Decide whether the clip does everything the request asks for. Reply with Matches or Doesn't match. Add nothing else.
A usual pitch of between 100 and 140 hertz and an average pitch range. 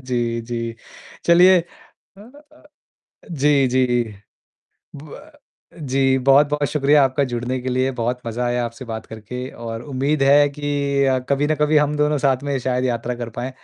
Matches